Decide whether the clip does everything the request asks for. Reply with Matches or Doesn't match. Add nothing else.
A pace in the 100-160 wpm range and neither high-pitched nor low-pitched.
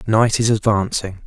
Doesn't match